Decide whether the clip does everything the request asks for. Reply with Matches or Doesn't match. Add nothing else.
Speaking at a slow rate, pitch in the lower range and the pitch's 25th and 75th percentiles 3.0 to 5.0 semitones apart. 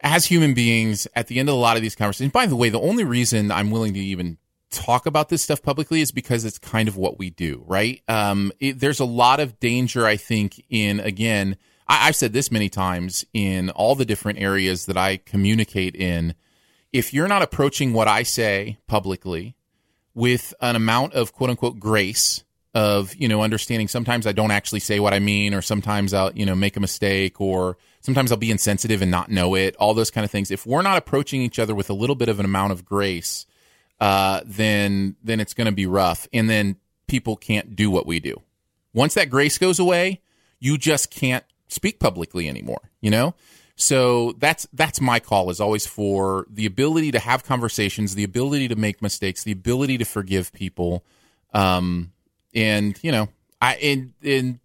Doesn't match